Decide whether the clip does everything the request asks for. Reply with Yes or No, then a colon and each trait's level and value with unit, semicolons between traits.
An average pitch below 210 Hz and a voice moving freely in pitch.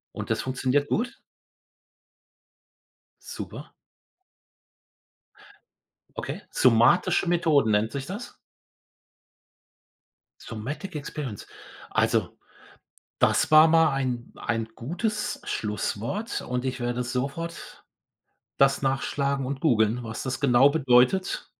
No: low, 135 Hz; average, 4.6 semitones